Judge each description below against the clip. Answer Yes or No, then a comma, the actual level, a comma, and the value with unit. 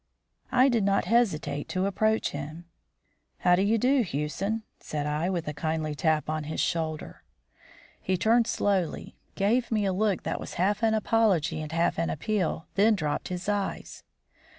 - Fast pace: No, average, 170 wpm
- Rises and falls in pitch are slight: No, wide, 5.5 semitones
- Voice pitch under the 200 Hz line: Yes, medium, 185 Hz